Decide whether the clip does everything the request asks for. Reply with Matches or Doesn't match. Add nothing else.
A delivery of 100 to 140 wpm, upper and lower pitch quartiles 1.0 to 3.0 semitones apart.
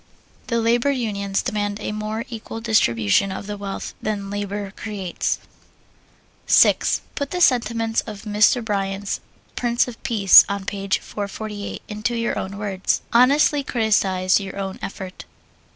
Matches